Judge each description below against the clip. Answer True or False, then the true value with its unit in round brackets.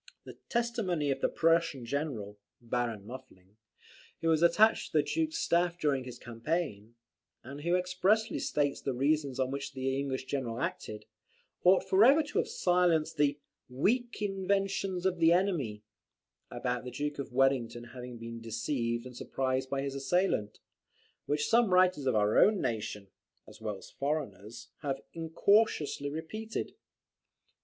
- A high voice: False (140 Hz)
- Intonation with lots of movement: True (6.7 semitones)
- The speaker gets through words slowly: False (150 wpm)